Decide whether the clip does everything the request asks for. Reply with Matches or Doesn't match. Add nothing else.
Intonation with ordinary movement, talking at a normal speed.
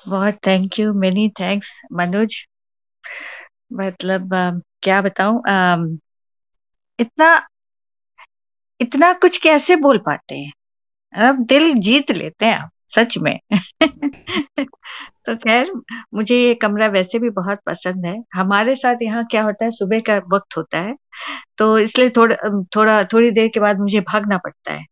Matches